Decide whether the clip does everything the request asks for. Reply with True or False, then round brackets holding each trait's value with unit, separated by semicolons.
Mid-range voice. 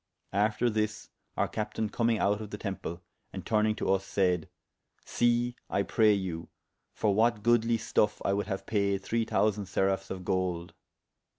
False (105 Hz)